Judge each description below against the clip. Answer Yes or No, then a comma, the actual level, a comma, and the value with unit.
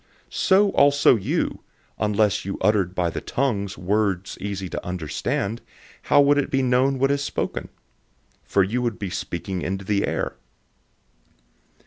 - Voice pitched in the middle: No, low, 105 Hz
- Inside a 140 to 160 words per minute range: Yes, average, 150 wpm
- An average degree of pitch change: No, wide, 5.8 semitones